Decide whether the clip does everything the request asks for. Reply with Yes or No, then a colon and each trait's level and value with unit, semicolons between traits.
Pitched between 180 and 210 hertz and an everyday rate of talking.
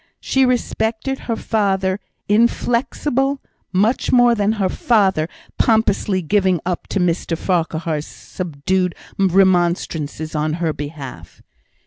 No: high, 190 Hz; slow, 105 wpm